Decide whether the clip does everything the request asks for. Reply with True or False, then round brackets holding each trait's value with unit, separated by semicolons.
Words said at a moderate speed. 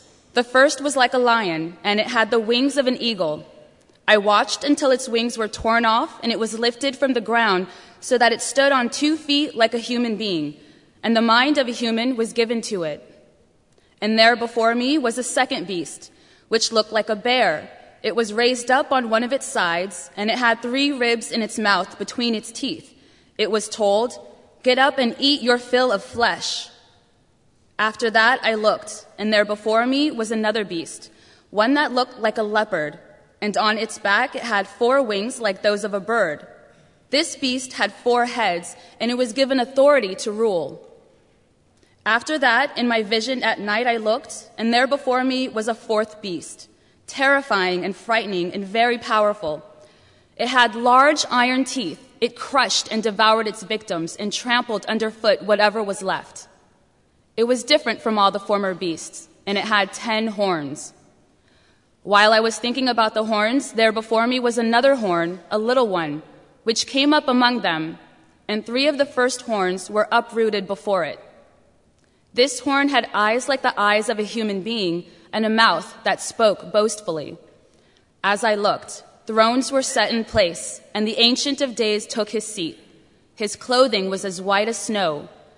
True (180 wpm)